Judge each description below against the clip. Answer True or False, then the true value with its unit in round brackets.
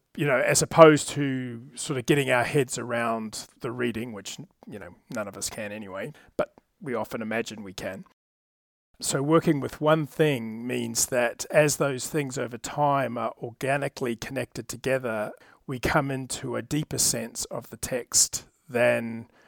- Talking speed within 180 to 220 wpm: False (165 wpm)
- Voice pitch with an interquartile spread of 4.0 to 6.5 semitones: False (3.4 semitones)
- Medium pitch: False (130 Hz)